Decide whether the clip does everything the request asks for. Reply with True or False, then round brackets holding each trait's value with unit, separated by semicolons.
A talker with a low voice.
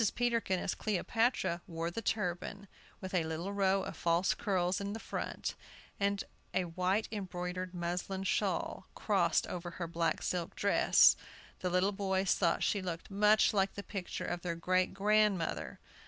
False (185 Hz)